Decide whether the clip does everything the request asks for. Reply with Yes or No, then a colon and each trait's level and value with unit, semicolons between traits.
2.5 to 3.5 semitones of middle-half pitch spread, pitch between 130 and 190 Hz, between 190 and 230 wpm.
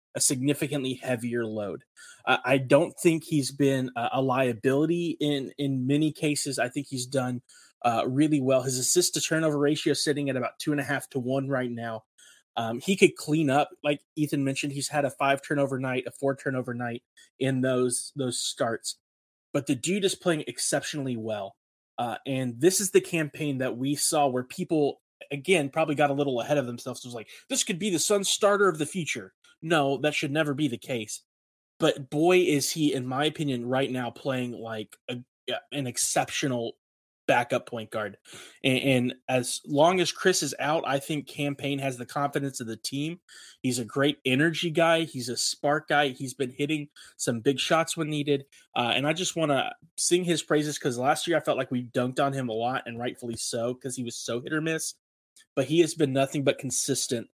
Yes: average, 3.1 semitones; medium, 140 Hz; fast, 205 wpm